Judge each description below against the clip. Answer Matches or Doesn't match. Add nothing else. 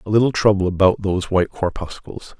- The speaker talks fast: Doesn't match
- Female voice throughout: Doesn't match